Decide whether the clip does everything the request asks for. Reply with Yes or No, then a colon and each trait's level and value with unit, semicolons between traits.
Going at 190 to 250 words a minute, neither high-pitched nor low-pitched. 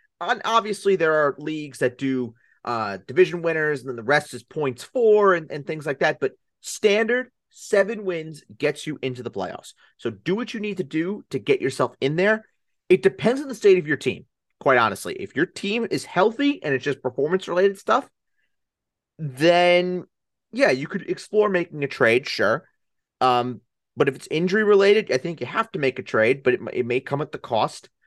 Yes: average, 200 wpm; medium, 170 Hz